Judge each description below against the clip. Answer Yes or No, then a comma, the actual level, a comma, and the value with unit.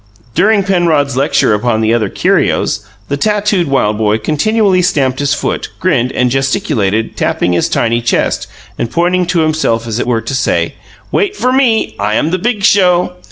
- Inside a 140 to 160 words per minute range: No, average, 175 wpm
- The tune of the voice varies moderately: No, wide, 8.2 semitones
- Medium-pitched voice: Yes, medium, 145 Hz